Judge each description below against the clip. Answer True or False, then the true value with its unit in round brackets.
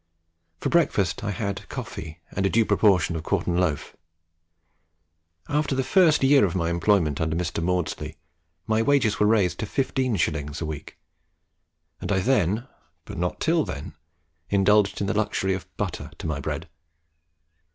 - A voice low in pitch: True (95 Hz)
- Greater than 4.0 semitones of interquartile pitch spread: True (5.0 semitones)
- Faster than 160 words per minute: False (155 wpm)